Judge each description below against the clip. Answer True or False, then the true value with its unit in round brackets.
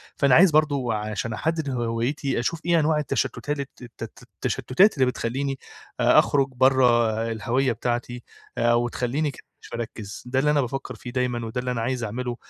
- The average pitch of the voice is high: False (125 Hz)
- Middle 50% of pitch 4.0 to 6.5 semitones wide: False (3.0 semitones)